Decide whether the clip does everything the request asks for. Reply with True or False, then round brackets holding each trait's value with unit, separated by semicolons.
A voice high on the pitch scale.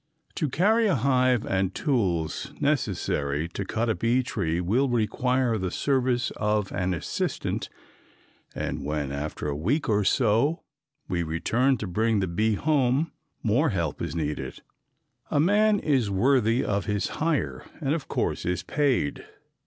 False (110 Hz)